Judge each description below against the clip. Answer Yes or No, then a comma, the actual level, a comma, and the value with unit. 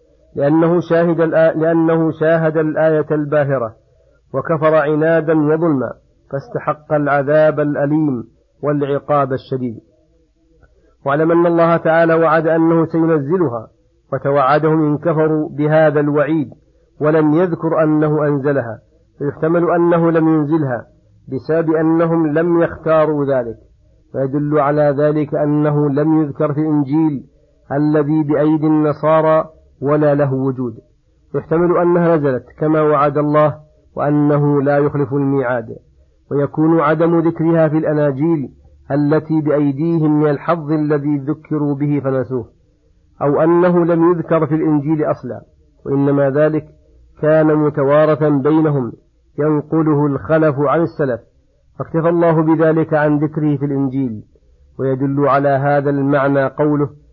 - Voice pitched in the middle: Yes, medium, 150 Hz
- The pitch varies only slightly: Yes, narrow, 1.9 semitones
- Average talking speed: Yes, average, 110 wpm